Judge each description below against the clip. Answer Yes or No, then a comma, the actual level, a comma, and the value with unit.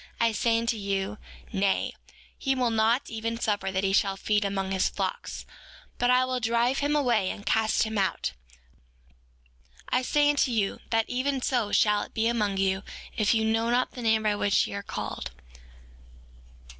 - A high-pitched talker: Yes, high, 220 Hz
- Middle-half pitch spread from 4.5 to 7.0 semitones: No, average, 3.2 semitones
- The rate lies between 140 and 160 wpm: No, average, 175 wpm